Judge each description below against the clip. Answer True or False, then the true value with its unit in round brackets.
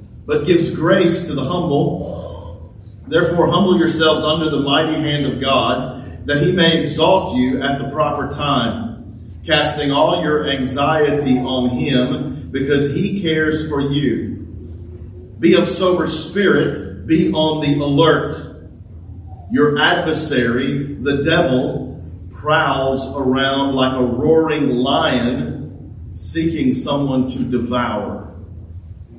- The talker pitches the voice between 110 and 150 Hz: True (140 Hz)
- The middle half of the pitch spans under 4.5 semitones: False (4.8 semitones)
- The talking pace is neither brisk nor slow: False (115 wpm)